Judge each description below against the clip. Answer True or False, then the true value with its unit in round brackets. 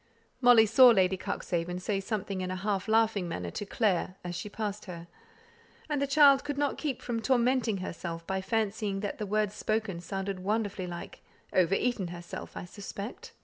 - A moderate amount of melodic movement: True (3.5 semitones)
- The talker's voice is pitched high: True (205 Hz)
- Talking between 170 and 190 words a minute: True (180 wpm)